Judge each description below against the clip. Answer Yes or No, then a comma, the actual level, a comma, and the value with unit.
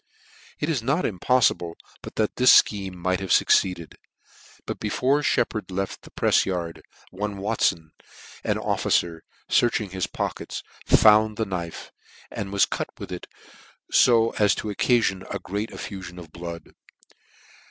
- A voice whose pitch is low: Yes, low, 100 Hz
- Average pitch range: Yes, average, 3.6 semitones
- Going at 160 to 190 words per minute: No, average, 140 wpm